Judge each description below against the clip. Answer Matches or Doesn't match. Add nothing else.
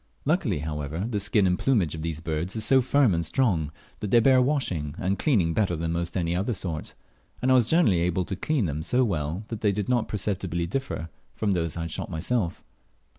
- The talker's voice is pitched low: Matches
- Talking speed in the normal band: Doesn't match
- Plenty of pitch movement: Matches